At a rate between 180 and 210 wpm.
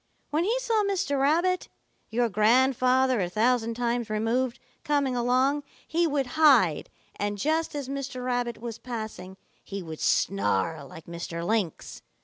No: average, 140 wpm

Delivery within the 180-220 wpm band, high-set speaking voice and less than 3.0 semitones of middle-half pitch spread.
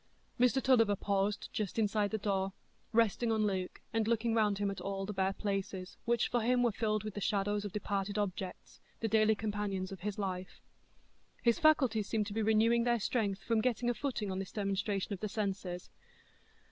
Yes: average, 190 wpm; high, 210 Hz; narrow, 2.4 semitones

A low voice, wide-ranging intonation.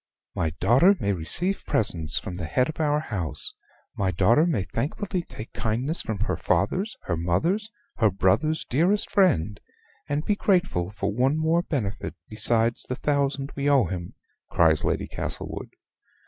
Yes: low, 125 Hz; wide, 8.6 semitones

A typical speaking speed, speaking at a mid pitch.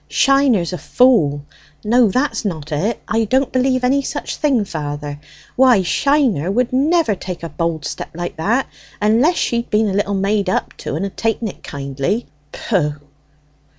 No: average, 165 wpm; high, 210 Hz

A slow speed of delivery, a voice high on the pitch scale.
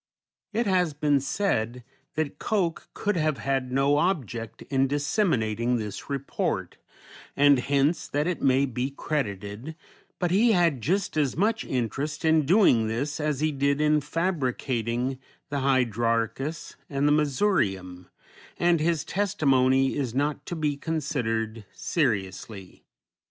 No: slow, 130 wpm; medium, 140 Hz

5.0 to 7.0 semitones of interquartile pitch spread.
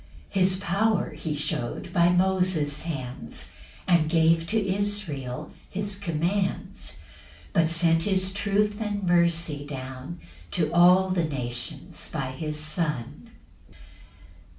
No: average, 4.2 semitones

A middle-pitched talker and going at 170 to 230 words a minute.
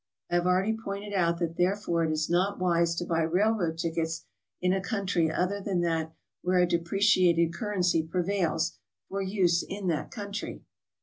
Yes: medium, 180 Hz; average, 175 wpm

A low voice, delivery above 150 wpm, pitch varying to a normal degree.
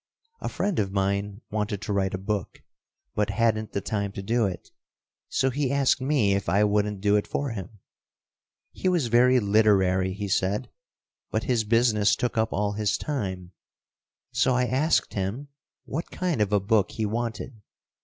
Yes: low, 105 Hz; average, 175 wpm; average, 3.5 semitones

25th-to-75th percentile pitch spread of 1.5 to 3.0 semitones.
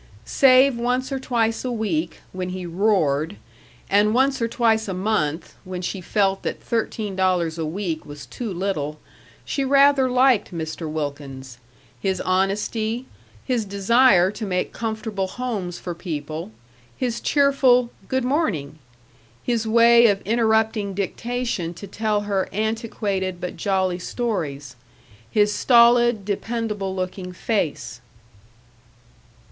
No: average, 4.7 semitones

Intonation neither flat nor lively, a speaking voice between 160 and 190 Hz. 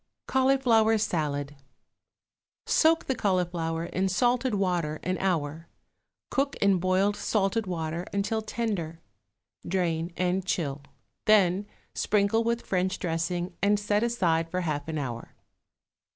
Yes: average, 4.3 semitones; medium, 185 Hz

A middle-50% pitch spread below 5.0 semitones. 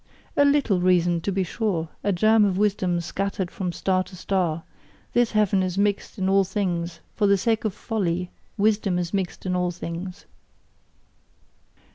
Yes: narrow, 2.5 semitones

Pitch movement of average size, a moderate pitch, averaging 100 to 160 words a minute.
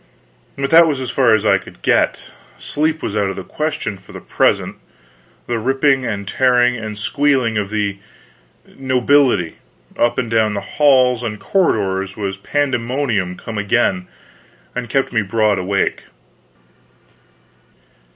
No: average, 4.8 semitones; low, 115 Hz; average, 140 wpm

